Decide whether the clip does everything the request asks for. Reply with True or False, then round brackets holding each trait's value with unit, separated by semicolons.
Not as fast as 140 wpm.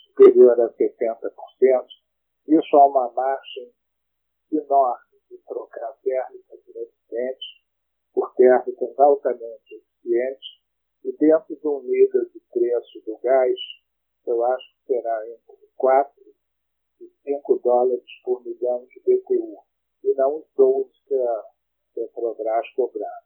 True (120 wpm)